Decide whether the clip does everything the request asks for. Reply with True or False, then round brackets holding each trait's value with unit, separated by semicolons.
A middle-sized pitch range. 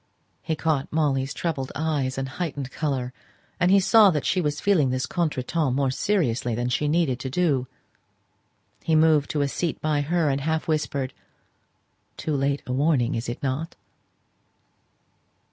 True (3.4 semitones)